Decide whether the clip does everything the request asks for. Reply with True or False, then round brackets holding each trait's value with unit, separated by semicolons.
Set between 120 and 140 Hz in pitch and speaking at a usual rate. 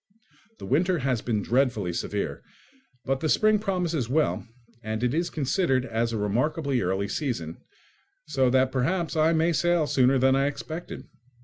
True (135 Hz; 155 wpm)